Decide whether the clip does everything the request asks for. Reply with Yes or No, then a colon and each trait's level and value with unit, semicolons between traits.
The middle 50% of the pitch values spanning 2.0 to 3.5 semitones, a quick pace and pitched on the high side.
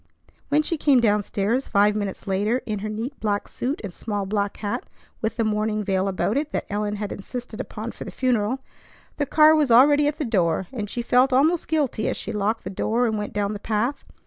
No: average, 4.0 semitones; fast, 225 wpm; high, 220 Hz